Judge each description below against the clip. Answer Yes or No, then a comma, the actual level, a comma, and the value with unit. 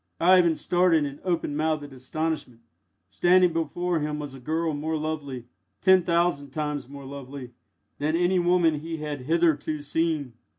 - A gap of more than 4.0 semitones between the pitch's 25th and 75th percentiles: No, average, 2.9 semitones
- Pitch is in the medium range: Yes, medium, 155 Hz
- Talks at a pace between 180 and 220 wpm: No, average, 145 wpm